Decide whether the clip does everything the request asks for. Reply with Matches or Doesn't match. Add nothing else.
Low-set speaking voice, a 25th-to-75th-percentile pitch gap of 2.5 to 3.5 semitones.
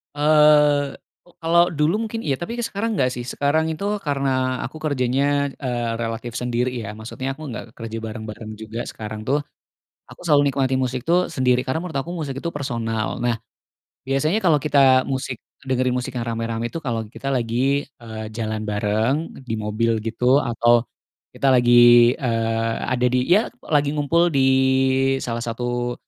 Doesn't match